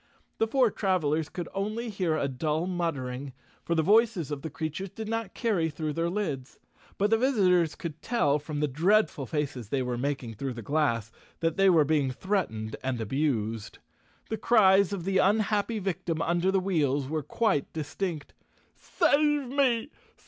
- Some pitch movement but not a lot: No, wide, 6.1 semitones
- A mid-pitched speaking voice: Yes, medium, 165 Hz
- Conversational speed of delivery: Yes, average, 170 wpm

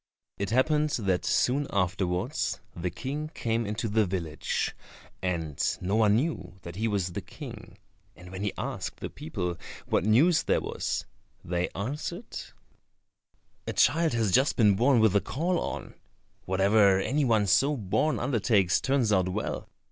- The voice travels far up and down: Yes, wide, 6.0 semitones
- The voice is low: Yes, low, 105 Hz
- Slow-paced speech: No, average, 155 wpm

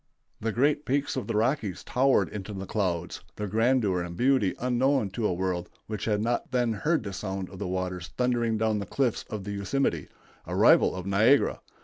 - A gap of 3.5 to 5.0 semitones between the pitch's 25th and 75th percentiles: Yes, average, 4.6 semitones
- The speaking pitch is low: Yes, low, 105 Hz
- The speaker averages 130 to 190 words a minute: No, average, 200 wpm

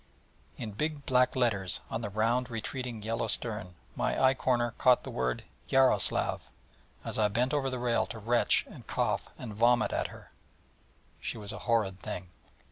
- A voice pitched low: Yes, low, 115 Hz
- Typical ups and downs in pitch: Yes, average, 3.0 semitones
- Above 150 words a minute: Yes, average, 170 wpm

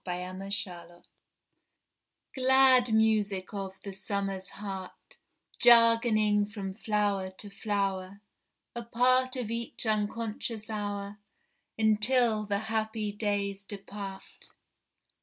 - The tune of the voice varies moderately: No, narrow, 2.2 semitones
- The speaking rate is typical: No, slow, 100 wpm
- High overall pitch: Yes, high, 210 Hz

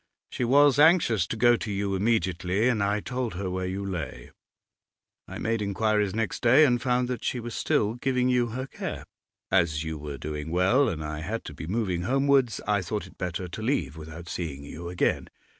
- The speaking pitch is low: Yes, low, 105 Hz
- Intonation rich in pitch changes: Yes, wide, 5.8 semitones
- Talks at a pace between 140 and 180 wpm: No, average, 200 wpm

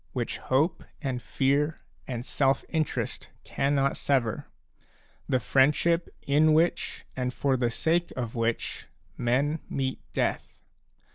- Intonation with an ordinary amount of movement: Yes, average, 3.3 semitones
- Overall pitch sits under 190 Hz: Yes, low, 135 Hz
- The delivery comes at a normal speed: No, slow, 120 wpm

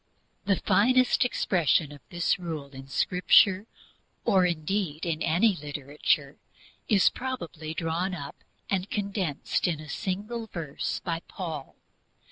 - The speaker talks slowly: Yes, slow, 125 wpm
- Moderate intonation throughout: Yes, average, 4.2 semitones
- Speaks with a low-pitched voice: No, medium, 175 Hz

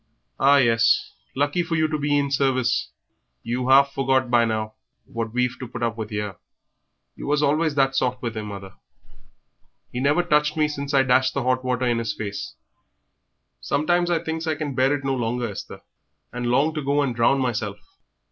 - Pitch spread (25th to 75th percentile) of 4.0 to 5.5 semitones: No, average, 3.4 semitones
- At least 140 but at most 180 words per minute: No, average, 195 wpm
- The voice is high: No, low, 130 Hz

